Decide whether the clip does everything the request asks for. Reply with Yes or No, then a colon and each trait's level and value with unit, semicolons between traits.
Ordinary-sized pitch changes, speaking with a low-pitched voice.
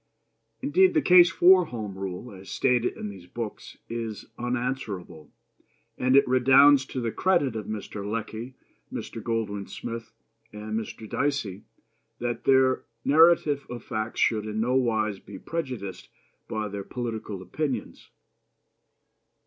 Yes: average, 3.9 semitones; low, 115 Hz